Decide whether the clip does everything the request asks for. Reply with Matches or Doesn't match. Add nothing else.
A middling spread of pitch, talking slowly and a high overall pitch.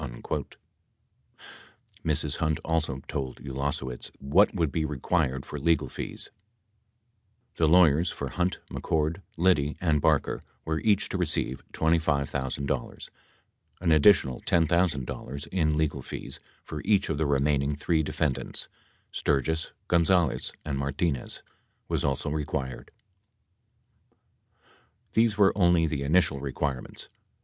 Doesn't match